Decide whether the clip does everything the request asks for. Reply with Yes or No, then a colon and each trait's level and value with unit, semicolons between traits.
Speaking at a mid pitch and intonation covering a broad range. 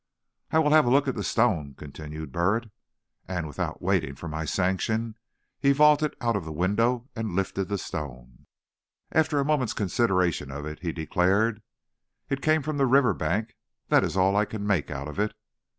No: low, 100 Hz; wide, 7.5 semitones